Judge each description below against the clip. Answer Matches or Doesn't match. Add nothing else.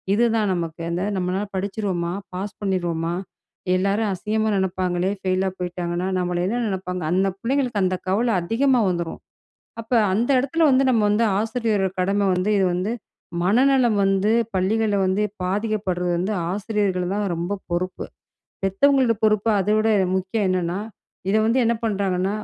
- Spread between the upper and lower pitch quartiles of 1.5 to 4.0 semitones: Matches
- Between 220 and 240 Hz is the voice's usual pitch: Doesn't match